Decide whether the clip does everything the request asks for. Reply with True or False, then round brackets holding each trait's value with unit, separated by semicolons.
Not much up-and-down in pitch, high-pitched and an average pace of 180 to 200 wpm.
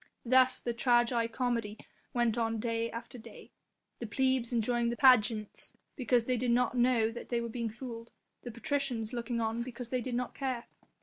True (1.5 semitones; 235 Hz; 185 wpm)